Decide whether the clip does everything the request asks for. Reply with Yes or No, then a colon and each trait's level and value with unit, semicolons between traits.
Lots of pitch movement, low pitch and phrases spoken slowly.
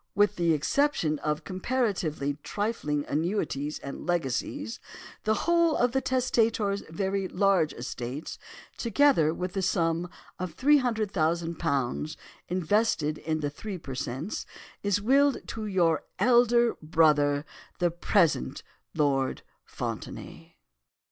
No: wide, 6.3 semitones; medium, 180 Hz; slow, 110 wpm